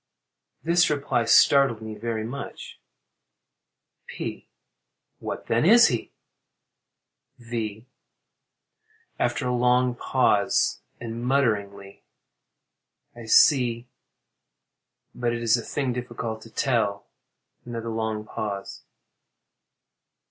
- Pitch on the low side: Yes, low, 115 Hz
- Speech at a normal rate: No, slow, 90 wpm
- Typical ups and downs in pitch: No, narrow, 2.1 semitones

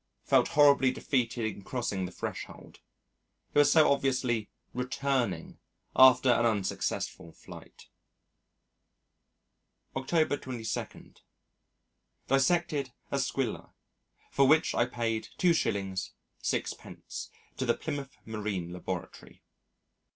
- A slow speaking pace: Yes, slow, 95 wpm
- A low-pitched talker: Yes, low, 125 Hz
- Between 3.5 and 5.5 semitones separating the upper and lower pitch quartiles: Yes, average, 3.9 semitones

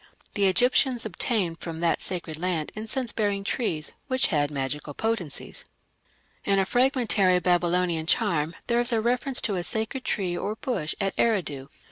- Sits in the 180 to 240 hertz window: Yes, high, 190 Hz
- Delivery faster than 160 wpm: No, average, 155 wpm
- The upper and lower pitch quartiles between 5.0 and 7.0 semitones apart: Yes, wide, 5.5 semitones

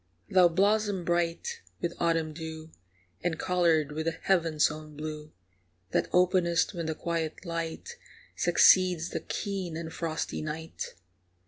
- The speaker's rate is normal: No, slow, 130 wpm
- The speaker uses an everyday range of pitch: No, narrow, 2.3 semitones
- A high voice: No, medium, 165 Hz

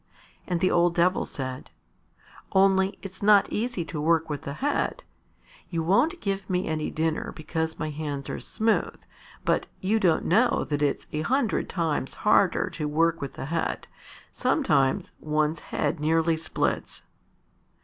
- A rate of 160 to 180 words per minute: No, average, 150 wpm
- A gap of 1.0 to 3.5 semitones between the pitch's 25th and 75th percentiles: No, average, 4.0 semitones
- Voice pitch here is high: No, medium, 165 Hz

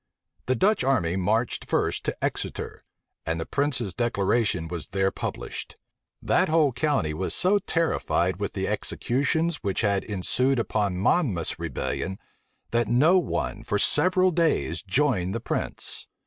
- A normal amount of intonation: No, wide, 7.6 semitones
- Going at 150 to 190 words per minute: No, average, 140 wpm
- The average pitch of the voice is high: No, low, 115 Hz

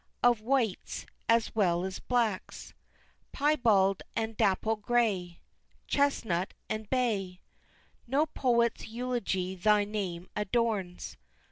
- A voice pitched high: Yes, high, 215 Hz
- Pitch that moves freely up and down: No, average, 4.1 semitones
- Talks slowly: Yes, slow, 100 wpm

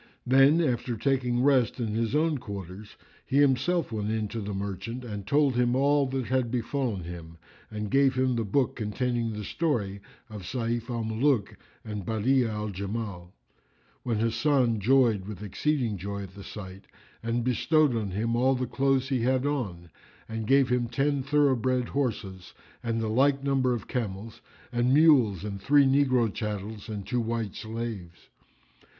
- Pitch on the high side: No, low, 115 Hz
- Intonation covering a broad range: No, average, 4.0 semitones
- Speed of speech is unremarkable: Yes, average, 165 wpm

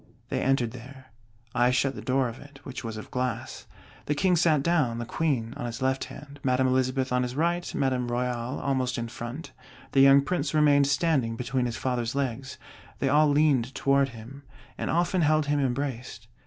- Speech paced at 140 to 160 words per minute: No, average, 190 wpm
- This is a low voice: Yes, low, 130 Hz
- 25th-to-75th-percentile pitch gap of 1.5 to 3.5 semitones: Yes, average, 2.7 semitones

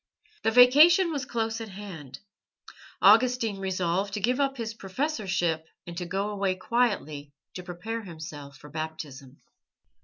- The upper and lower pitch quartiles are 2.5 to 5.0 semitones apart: No, wide, 5.5 semitones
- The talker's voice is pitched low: No, high, 195 Hz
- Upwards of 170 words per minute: No, average, 140 wpm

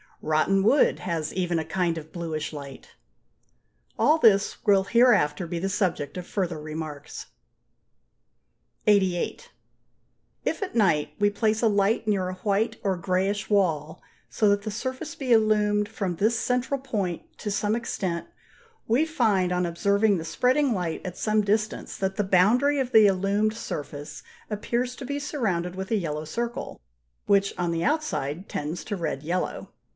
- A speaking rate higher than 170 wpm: No, average, 160 wpm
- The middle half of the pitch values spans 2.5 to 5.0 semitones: Yes, average, 4.3 semitones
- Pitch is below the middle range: No, high, 195 Hz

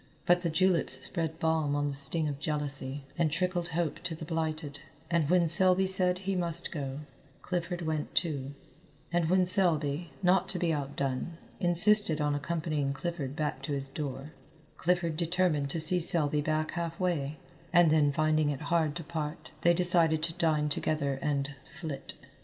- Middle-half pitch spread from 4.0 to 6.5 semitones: No, average, 3.0 semitones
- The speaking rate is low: No, average, 170 wpm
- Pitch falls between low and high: Yes, medium, 160 Hz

